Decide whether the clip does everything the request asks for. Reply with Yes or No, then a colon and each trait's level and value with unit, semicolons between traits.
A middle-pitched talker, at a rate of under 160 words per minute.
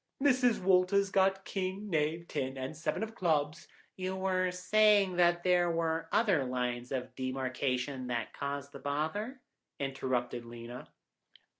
Yes: medium, 165 Hz; average, 140 wpm